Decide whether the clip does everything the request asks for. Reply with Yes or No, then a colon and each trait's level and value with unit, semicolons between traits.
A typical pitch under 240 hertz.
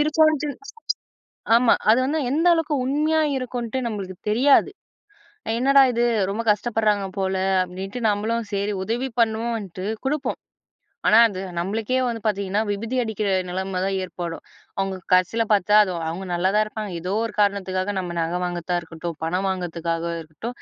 Yes: high, 205 Hz